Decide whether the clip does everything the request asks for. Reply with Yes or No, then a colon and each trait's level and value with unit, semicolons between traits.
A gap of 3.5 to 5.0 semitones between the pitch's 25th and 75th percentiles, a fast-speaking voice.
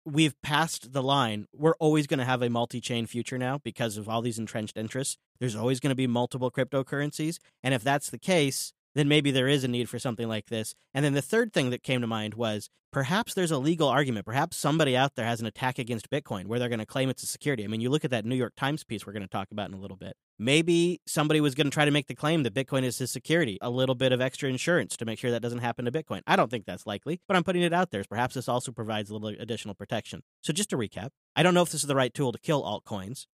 Yes: average, 4.1 semitones; fast, 285 wpm